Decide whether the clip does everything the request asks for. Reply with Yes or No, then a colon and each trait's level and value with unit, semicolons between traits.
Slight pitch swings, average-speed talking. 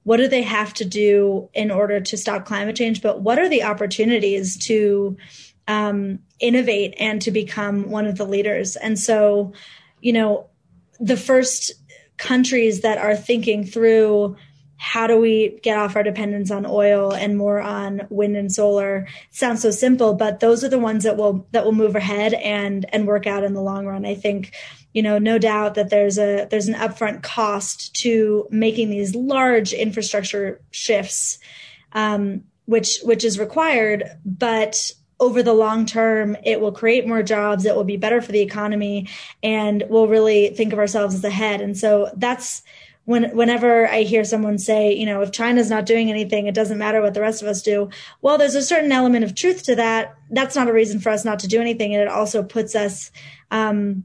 Yes: narrow, 1.7 semitones; average, 195 wpm